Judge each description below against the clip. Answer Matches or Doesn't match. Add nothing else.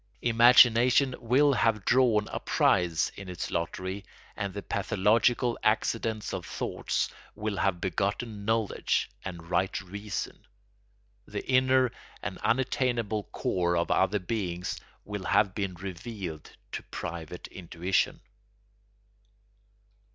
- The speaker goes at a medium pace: Doesn't match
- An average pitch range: Matches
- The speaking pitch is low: Matches